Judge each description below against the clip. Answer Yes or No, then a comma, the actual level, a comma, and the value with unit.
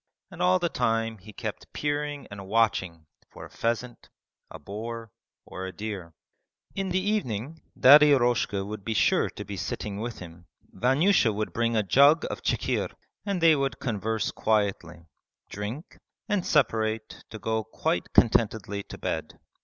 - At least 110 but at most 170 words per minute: Yes, average, 155 wpm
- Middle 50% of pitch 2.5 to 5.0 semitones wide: No, wide, 5.4 semitones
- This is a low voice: Yes, low, 115 Hz